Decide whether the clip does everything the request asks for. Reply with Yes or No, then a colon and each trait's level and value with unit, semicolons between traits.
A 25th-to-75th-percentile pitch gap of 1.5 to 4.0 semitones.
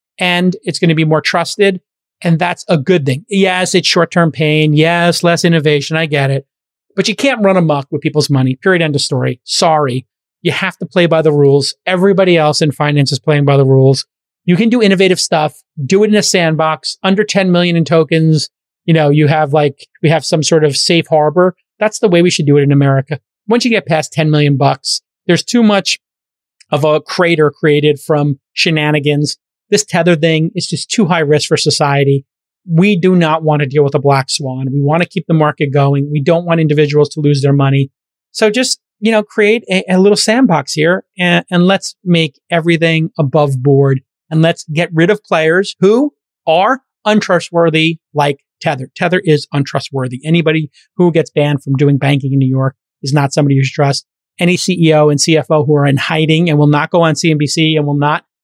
Yes: average, 3.6 semitones